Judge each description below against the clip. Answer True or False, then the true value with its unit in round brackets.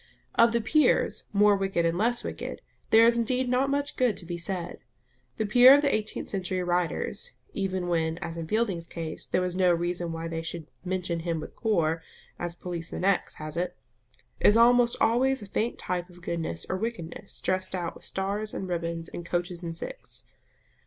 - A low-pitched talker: False (185 Hz)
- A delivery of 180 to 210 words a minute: True (190 wpm)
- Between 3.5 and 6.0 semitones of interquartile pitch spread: True (4.6 semitones)